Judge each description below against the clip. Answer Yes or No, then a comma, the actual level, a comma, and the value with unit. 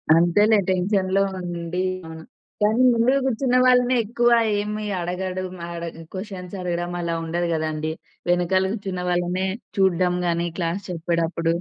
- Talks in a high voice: No, medium, 180 Hz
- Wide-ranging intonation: No, average, 2.9 semitones